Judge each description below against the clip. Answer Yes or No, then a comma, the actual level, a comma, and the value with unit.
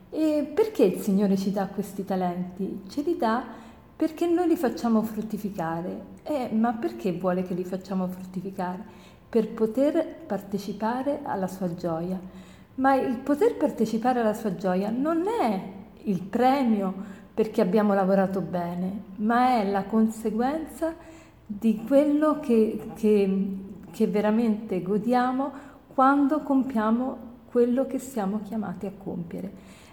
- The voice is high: Yes, high, 220 Hz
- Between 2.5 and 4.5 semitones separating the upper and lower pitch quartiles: No, average, 5.1 semitones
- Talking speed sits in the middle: Yes, average, 130 wpm